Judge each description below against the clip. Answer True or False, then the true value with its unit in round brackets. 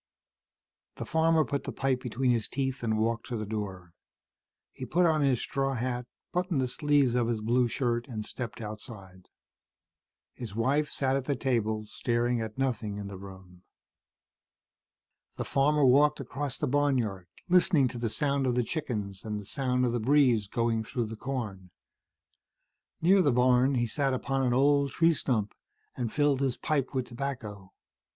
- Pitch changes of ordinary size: True (3.9 semitones)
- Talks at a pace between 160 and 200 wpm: True (170 wpm)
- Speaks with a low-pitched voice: True (125 Hz)